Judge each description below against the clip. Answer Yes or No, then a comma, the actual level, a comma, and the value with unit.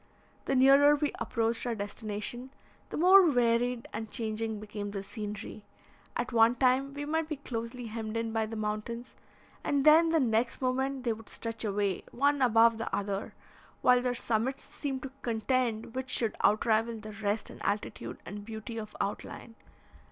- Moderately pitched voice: No, high, 230 Hz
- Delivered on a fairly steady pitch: No, average, 3.1 semitones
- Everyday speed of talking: Yes, average, 165 wpm